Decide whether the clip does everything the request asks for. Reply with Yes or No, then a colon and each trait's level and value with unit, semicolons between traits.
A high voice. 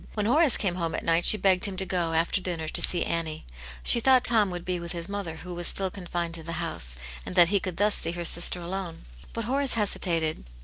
No: medium, 180 Hz